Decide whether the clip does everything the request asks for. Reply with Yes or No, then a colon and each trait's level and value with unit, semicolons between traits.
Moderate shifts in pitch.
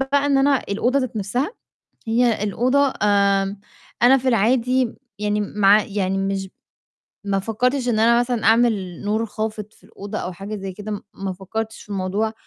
Yes: average, 3.6 semitones